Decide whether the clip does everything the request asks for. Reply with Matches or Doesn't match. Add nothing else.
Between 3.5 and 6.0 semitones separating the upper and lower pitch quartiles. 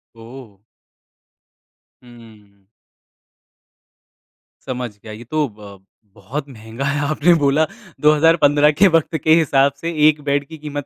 Matches